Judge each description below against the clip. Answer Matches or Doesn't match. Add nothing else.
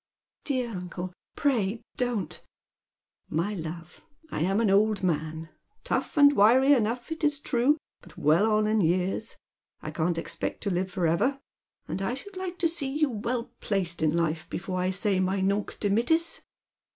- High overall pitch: Matches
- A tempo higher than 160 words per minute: Matches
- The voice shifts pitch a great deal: Matches